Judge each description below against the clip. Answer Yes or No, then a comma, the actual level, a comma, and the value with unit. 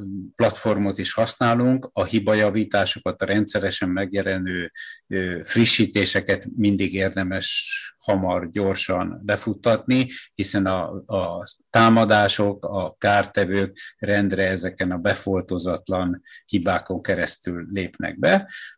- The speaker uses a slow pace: Yes, slow, 95 wpm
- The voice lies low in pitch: Yes, low, 100 Hz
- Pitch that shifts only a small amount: Yes, narrow, 2.3 semitones